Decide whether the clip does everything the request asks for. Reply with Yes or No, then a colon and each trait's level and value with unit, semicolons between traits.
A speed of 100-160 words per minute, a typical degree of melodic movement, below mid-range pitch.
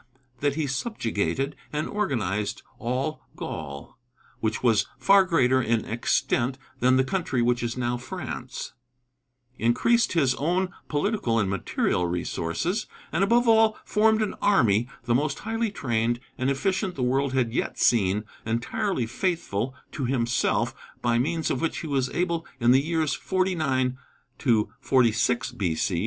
No: average, 140 wpm; wide, 6.5 semitones; low, 130 Hz